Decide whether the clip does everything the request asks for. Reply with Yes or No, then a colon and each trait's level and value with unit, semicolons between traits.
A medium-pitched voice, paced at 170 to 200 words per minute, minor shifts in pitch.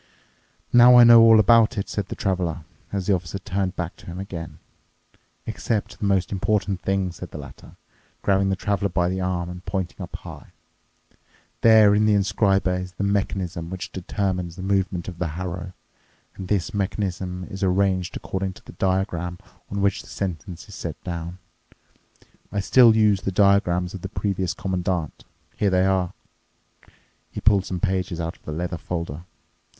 No: very low, 95 Hz; average, 175 wpm; narrow, 2.0 semitones